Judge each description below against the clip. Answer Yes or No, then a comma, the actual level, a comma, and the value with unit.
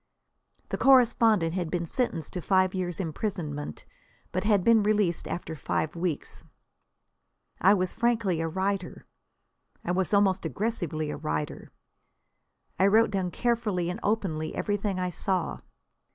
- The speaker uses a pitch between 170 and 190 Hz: Yes, medium, 185 Hz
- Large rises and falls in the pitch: No, average, 3.6 semitones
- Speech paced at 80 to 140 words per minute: Yes, slow, 135 wpm